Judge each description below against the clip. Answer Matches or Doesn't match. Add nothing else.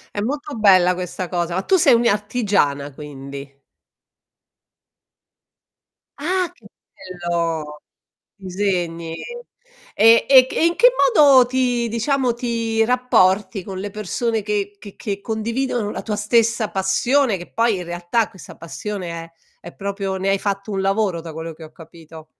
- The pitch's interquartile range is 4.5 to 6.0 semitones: Matches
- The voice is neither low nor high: Doesn't match